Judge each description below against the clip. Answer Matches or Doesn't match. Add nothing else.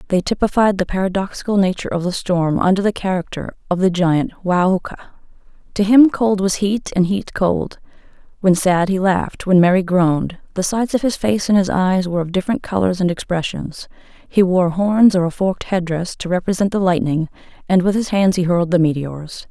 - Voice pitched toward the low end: Doesn't match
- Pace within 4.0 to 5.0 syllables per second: Doesn't match